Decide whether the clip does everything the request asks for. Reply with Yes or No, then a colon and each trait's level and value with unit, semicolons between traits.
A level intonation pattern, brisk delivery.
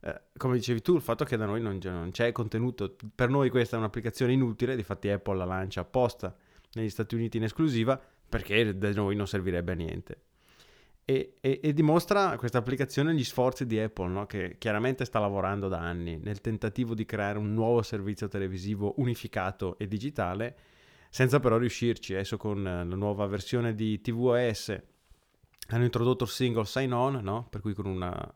No: average, 3.6 semitones; fast, 180 wpm